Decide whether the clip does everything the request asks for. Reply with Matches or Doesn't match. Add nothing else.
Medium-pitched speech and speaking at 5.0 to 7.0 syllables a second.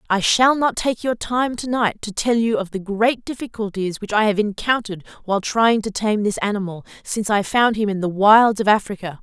Doesn't match